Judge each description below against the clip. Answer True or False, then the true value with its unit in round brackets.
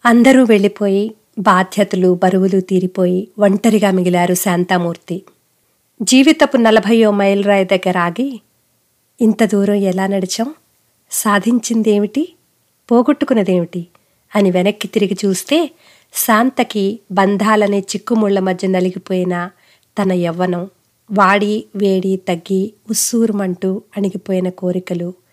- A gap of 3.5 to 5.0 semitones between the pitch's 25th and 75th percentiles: False (3.0 semitones)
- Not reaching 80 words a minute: False (90 wpm)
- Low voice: False (200 Hz)